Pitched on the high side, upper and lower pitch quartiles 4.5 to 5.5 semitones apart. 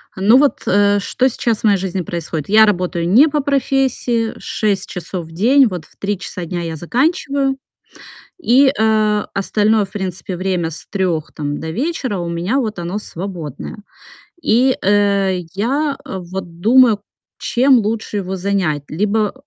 Yes: high, 205 Hz; average, 5.0 semitones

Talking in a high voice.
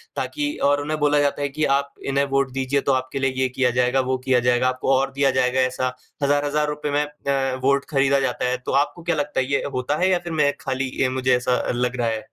No: low, 135 Hz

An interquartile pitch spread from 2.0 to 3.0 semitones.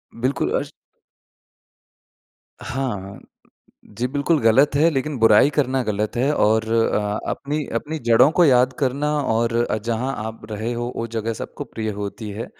No: average, 3.6 semitones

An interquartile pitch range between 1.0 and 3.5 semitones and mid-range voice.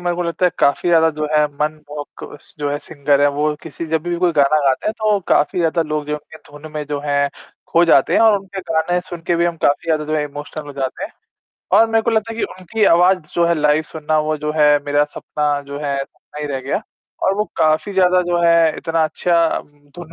Yes: average, 2.9 semitones; medium, 160 Hz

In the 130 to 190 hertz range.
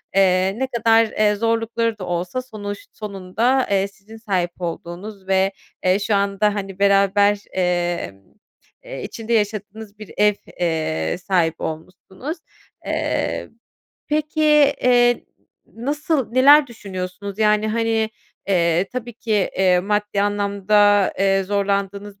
No: high, 205 Hz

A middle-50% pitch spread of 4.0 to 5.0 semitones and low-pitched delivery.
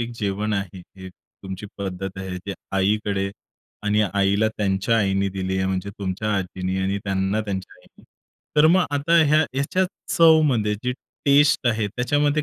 Yes: average, 4.7 semitones; low, 100 Hz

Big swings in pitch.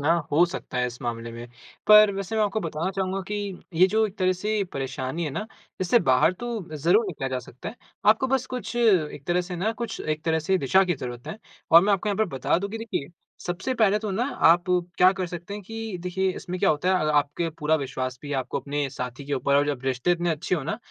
Yes: wide, 5.8 semitones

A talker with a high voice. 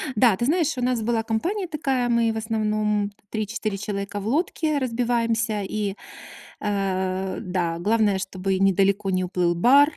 Yes: high, 215 Hz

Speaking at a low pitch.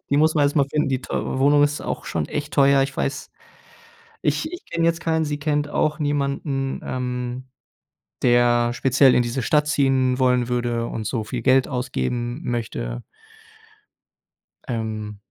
Yes: low, 130 Hz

